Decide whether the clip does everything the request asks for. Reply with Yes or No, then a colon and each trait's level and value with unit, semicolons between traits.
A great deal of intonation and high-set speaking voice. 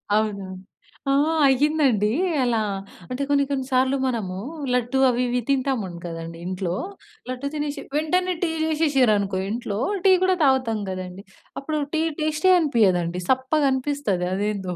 Yes: wide, 6.2 semitones; very high, 255 Hz